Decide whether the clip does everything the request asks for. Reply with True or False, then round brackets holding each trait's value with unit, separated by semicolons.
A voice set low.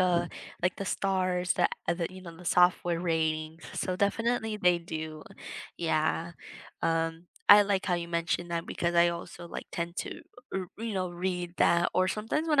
False (175 Hz)